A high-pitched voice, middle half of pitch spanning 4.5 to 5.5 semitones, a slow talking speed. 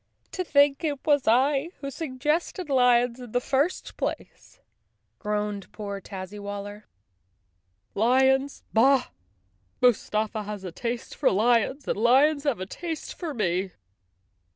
Yes: high, 245 Hz; average, 5.1 semitones; slow, 130 wpm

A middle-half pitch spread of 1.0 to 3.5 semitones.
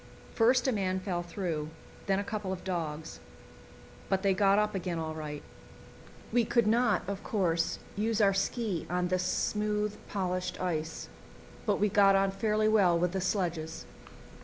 Yes: average, 3.1 semitones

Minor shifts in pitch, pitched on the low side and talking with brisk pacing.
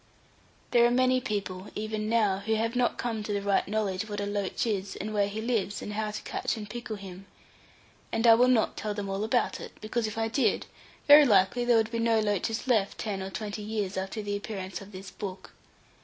No: narrow, 2.1 semitones; high, 215 Hz; fast, 225 wpm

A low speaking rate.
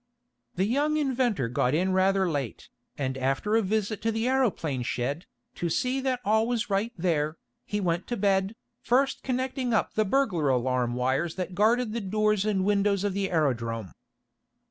No: average, 170 wpm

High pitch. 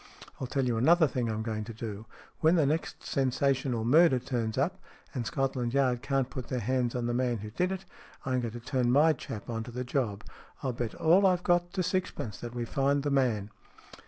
No: low, 125 Hz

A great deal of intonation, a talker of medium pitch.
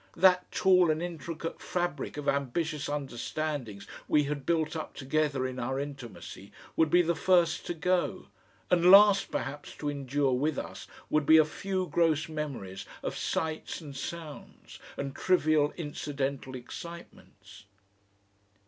No: average, 3.6 semitones; medium, 150 Hz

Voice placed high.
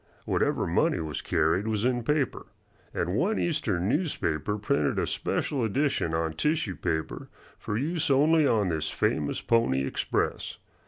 No: low, 105 Hz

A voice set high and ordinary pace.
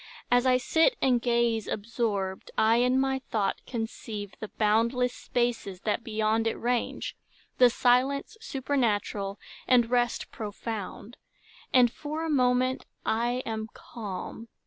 No: high, 235 Hz; slow, 125 wpm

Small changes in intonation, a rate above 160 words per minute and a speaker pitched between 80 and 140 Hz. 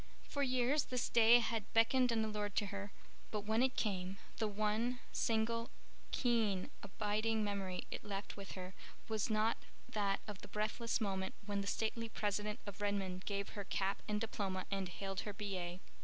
No: narrow, 2.3 semitones; average, 170 wpm; high, 210 Hz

